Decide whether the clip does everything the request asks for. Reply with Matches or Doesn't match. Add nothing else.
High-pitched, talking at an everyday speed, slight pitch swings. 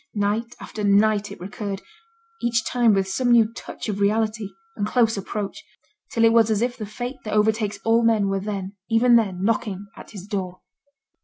Matches